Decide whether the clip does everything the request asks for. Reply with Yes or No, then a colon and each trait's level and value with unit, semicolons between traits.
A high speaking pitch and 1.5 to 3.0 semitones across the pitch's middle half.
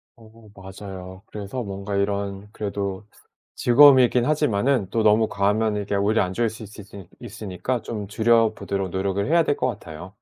No: low, 105 Hz; average, 2.7 semitones